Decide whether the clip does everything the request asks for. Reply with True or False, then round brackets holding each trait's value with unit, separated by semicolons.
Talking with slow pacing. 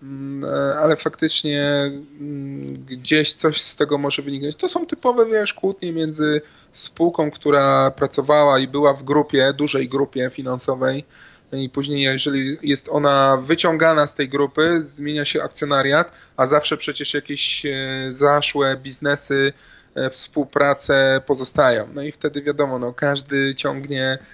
False (125 wpm)